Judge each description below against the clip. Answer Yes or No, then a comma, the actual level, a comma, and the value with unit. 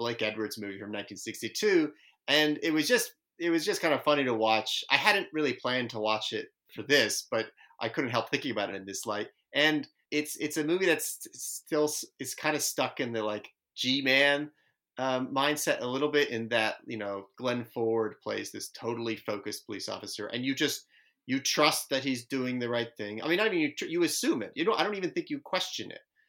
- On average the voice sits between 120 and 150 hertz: Yes, low, 135 Hz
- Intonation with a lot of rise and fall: Yes, wide, 5.7 semitones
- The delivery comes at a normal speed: No, fast, 220 wpm